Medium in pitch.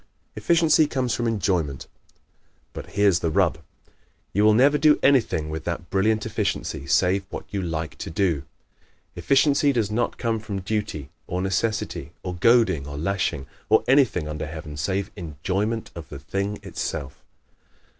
No: low, 100 Hz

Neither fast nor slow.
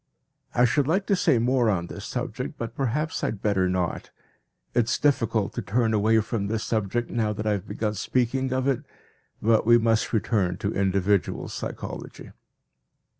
Yes: average, 175 wpm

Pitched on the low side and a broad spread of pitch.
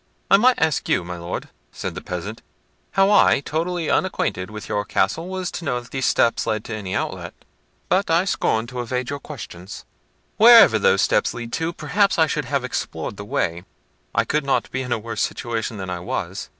Yes: low, 125 Hz; wide, 8.0 semitones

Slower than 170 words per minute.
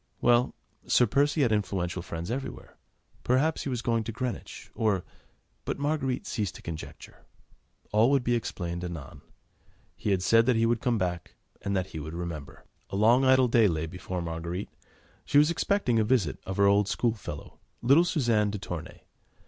No: average, 175 wpm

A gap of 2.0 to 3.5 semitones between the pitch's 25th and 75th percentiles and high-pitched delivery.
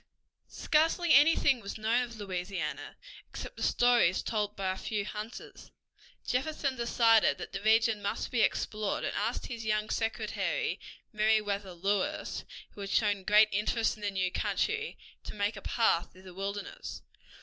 Yes: average, 2.9 semitones; high, 215 Hz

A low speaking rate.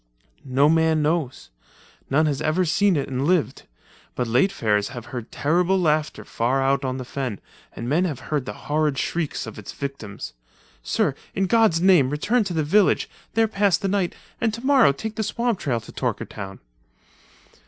No: average, 175 wpm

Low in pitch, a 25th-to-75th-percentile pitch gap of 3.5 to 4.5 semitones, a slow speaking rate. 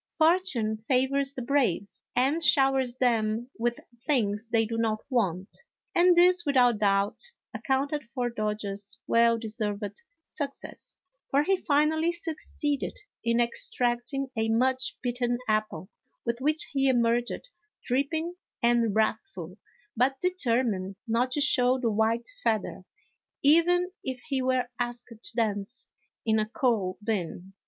No: high, 245 Hz; average, 4.0 semitones; slow, 130 wpm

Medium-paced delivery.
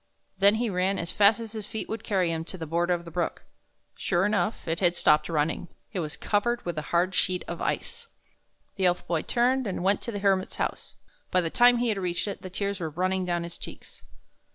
No: fast, 230 wpm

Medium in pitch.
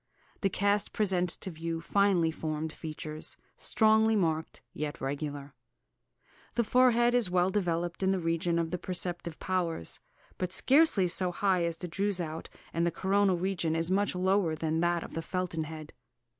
Yes: medium, 175 Hz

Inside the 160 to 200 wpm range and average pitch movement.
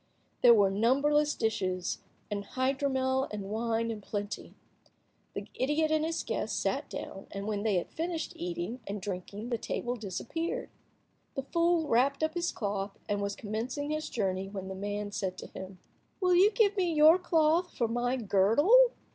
No: average, 170 wpm; wide, 7.5 semitones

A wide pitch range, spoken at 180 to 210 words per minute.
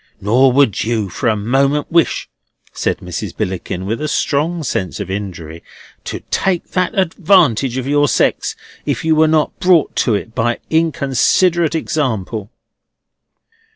No: wide, 6.8 semitones; average, 145 wpm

